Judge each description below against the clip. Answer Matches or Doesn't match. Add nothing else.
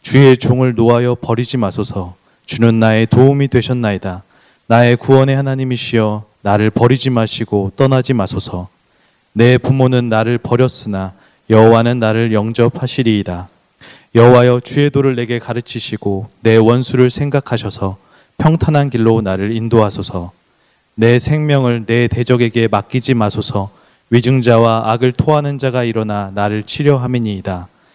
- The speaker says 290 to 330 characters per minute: Matches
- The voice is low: Matches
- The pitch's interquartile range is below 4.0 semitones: Matches